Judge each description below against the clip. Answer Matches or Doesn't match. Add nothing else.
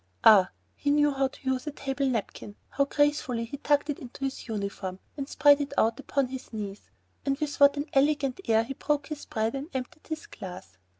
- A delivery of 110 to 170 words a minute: Doesn't match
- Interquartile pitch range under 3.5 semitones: Doesn't match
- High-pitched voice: Matches